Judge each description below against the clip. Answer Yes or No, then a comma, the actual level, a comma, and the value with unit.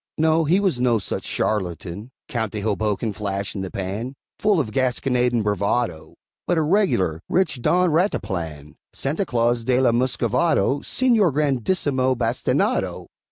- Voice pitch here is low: Yes, low, 125 Hz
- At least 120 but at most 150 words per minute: Yes, average, 145 wpm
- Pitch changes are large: Yes, wide, 6.6 semitones